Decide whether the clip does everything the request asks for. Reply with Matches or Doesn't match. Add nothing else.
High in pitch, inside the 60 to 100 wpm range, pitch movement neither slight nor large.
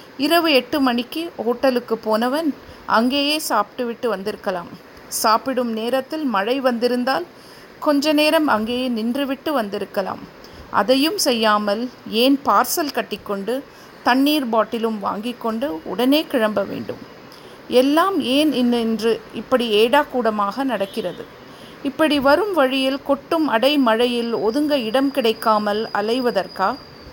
Matches